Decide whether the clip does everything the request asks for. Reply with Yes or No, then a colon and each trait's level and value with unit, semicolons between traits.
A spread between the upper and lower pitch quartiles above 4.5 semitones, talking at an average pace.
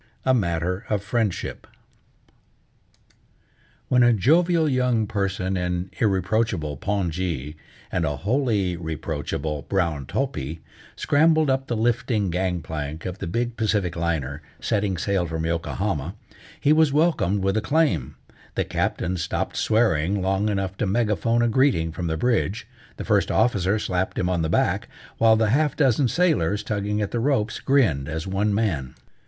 Yes: wide, 5.6 semitones; average, 150 wpm